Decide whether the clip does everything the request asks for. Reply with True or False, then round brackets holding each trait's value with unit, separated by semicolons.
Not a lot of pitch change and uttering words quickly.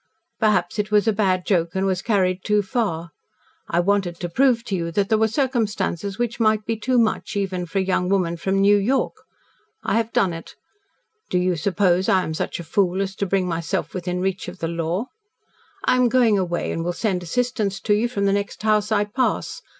False (3.3 semitones; 215 wpm)